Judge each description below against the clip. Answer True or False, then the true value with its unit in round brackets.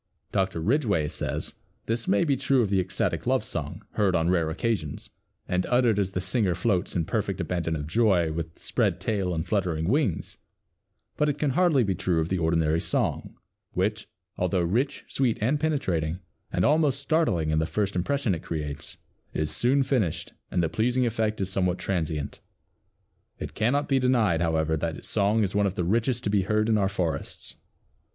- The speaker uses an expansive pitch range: True (5.9 semitones)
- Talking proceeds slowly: False (185 wpm)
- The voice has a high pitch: False (95 Hz)